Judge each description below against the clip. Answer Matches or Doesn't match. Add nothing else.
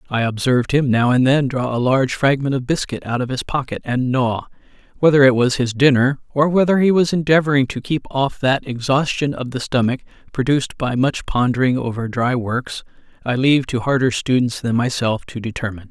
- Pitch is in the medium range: Doesn't match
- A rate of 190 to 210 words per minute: Matches